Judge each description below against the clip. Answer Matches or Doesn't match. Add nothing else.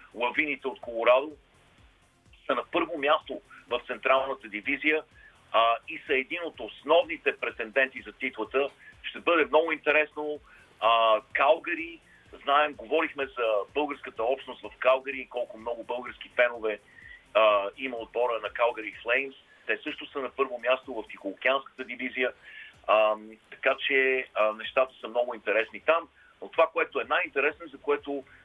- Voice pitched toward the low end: Matches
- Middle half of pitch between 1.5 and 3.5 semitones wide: Doesn't match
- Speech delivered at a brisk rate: Doesn't match